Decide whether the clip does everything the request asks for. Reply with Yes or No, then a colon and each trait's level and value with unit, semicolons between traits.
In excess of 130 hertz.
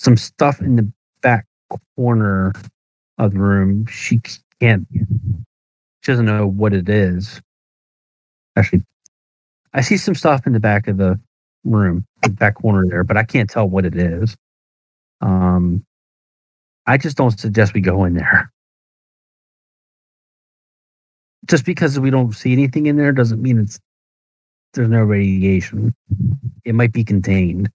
No: low, 110 Hz